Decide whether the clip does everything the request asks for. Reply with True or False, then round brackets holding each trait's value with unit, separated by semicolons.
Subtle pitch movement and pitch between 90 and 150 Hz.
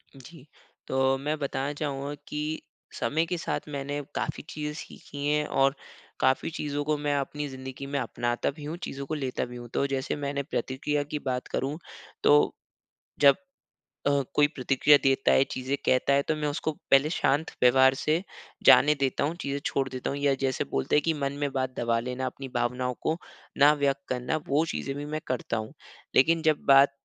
True (2.0 semitones; 140 Hz)